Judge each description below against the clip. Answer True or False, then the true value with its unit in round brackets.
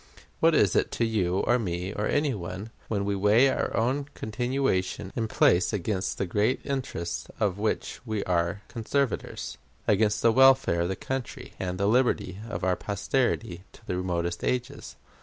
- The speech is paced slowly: False (170 wpm)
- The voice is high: False (105 Hz)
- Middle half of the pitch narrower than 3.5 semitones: False (4.9 semitones)